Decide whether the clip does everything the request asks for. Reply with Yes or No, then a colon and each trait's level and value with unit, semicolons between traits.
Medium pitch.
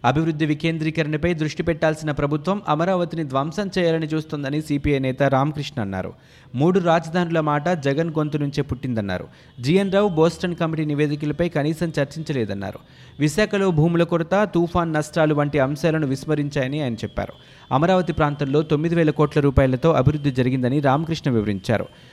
Yes: medium, 150 Hz